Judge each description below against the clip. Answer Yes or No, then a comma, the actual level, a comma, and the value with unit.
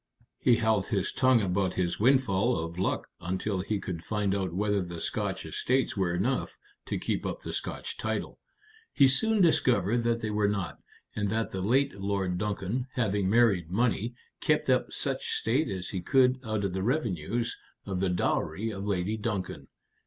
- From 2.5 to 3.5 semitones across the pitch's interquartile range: No, average, 3.9 semitones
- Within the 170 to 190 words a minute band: Yes, average, 175 wpm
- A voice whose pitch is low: Yes, low, 105 Hz